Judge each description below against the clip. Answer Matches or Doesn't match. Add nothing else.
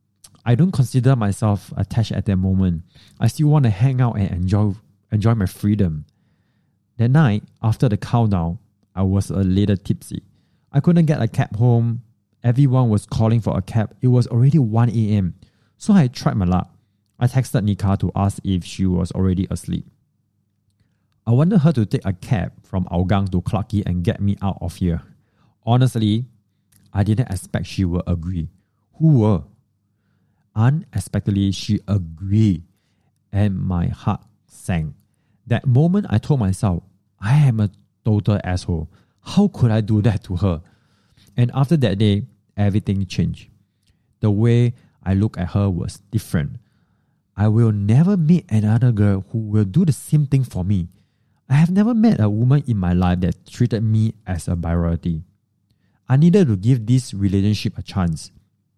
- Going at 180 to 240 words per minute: Doesn't match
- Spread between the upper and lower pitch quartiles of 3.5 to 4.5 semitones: Matches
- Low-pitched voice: Matches